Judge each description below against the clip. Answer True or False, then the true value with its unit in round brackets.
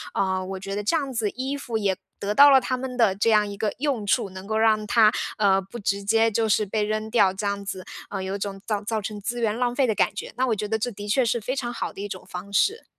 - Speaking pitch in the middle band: False (215 Hz)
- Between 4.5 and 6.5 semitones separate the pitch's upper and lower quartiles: False (3.0 semitones)